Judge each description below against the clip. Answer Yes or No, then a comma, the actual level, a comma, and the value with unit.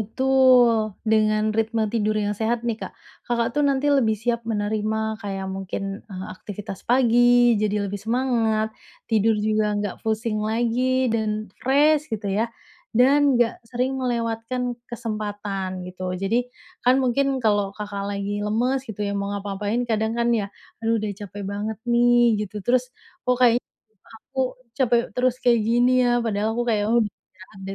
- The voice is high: Yes, high, 225 Hz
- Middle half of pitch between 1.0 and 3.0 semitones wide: Yes, average, 2.7 semitones